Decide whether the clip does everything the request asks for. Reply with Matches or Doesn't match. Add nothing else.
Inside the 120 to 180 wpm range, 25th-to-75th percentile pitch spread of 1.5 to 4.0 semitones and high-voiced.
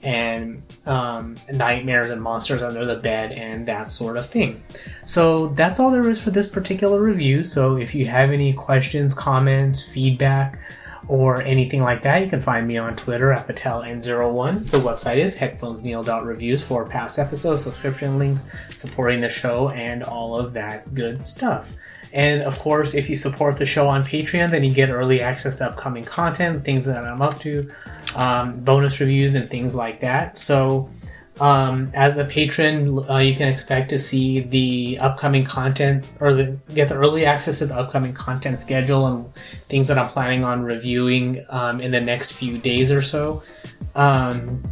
Doesn't match